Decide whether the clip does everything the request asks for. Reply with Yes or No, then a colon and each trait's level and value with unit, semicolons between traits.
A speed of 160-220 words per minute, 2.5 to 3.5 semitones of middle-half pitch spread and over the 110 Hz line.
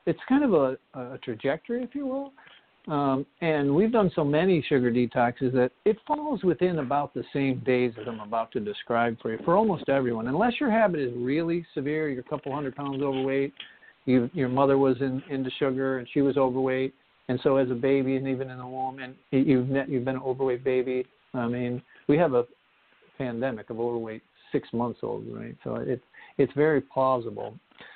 Yes: average, 200 wpm; average, 2.9 semitones; low, 135 Hz